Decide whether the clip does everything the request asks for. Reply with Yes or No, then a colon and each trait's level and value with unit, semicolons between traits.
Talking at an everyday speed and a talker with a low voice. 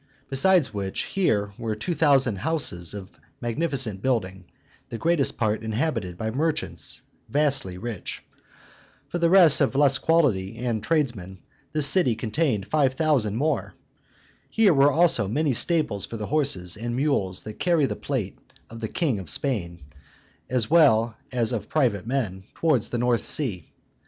Yes: average, 150 wpm; low, 125 Hz